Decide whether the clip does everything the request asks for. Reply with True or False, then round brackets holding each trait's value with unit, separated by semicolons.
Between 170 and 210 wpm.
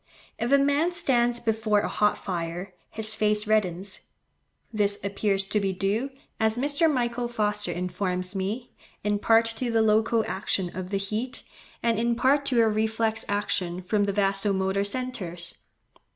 False (160 wpm)